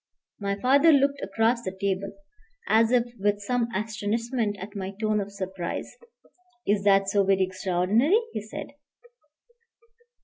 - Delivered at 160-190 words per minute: No, slow, 135 wpm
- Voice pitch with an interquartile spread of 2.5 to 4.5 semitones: Yes, average, 3.0 semitones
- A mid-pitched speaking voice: No, high, 205 Hz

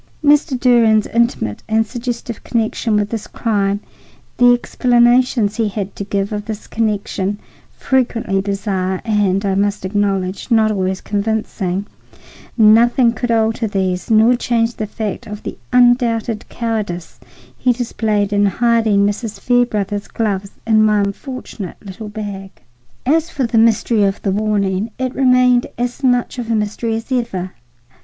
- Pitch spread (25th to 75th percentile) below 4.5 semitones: Yes, average, 2.9 semitones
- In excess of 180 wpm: No, average, 140 wpm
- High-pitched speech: Yes, high, 220 Hz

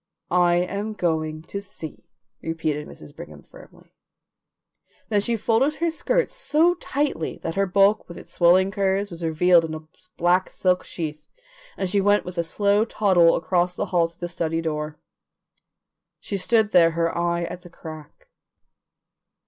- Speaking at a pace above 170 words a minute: No, average, 160 wpm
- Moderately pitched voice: Yes, medium, 180 Hz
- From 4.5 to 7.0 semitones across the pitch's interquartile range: No, average, 3.6 semitones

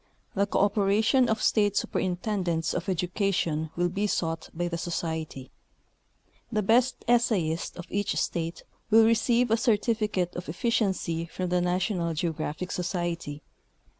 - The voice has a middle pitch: Yes, medium, 180 Hz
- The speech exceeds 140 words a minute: No, slow, 135 wpm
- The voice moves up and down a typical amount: Yes, average, 4.0 semitones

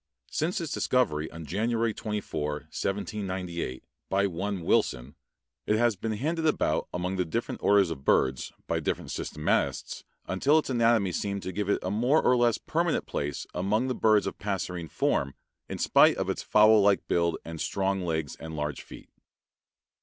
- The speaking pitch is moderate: No, low, 100 Hz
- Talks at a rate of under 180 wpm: Yes, average, 170 wpm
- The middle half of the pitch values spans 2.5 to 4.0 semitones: No, average, 5.1 semitones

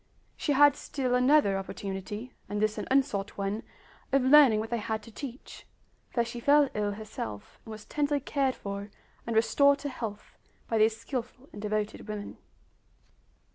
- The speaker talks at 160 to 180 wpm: Yes, average, 165 wpm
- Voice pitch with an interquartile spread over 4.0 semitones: Yes, average, 4.4 semitones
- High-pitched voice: Yes, high, 230 Hz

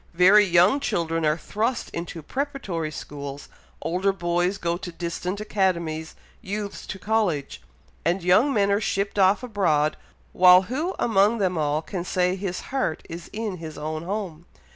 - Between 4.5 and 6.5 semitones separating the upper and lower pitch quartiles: No, average, 3.8 semitones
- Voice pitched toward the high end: No, medium, 180 Hz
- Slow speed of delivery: No, average, 155 wpm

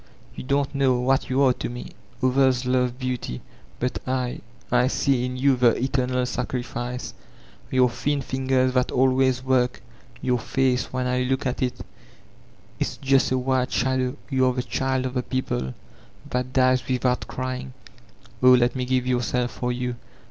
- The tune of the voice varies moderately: No, narrow, 0.8 semitones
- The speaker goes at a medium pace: Yes, average, 170 wpm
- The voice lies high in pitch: No, low, 130 Hz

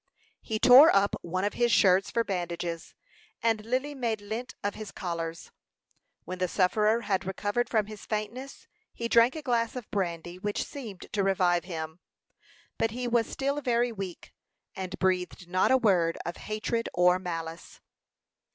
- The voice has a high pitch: Yes, high, 205 Hz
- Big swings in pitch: No, average, 4.4 semitones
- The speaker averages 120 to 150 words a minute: No, average, 165 wpm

